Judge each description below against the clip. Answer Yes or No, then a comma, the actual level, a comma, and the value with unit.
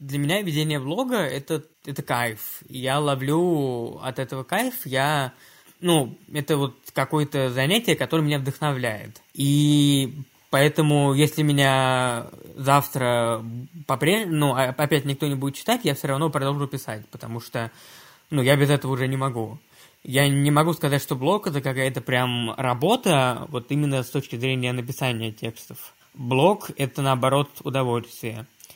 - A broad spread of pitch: No, narrow, 2.6 semitones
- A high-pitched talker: No, medium, 140 Hz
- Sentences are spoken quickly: No, average, 140 wpm